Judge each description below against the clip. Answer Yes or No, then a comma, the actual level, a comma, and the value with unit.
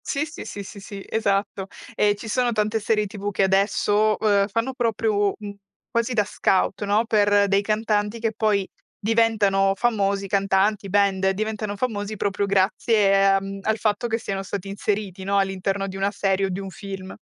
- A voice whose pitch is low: No, high, 205 Hz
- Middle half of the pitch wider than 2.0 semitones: No, narrow, 1.7 semitones